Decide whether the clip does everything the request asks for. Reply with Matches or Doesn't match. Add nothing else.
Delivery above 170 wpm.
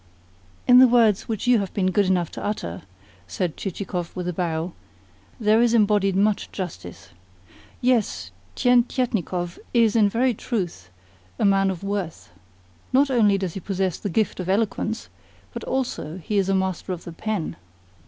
Doesn't match